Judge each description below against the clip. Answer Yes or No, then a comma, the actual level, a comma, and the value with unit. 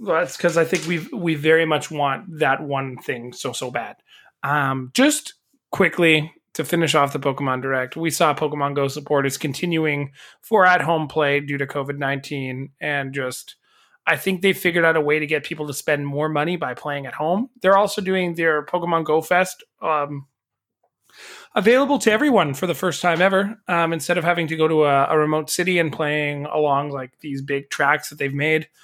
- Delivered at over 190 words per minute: Yes, average, 200 wpm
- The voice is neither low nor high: Yes, medium, 155 Hz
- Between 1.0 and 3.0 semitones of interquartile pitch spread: No, average, 3.6 semitones